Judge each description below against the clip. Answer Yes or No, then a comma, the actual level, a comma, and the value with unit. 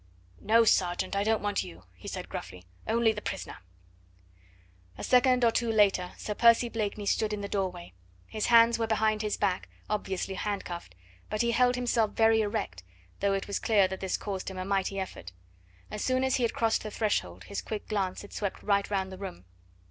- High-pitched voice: Yes, high, 205 Hz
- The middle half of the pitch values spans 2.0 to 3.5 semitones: Yes, average, 2.7 semitones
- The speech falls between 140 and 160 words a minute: No, average, 200 wpm